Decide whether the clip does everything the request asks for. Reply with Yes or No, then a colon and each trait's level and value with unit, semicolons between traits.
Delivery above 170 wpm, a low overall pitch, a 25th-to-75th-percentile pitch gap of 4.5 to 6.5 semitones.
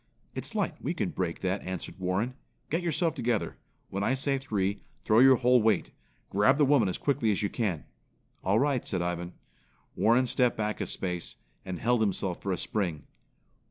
Yes: average, 185 wpm; low, 110 Hz; wide, 5.4 semitones